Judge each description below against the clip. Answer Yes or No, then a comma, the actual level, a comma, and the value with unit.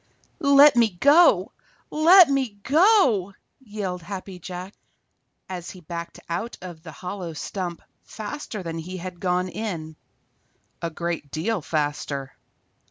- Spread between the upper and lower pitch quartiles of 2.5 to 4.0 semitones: No, average, 5.1 semitones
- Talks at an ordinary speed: No, slow, 130 wpm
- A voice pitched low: No, medium, 185 Hz